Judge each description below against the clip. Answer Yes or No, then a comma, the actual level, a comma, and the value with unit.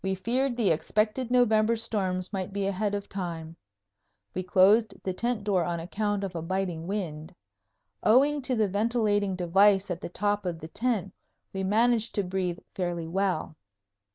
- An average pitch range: Yes, average, 3.1 semitones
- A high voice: Yes, high, 195 Hz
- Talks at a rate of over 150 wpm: Yes, average, 165 wpm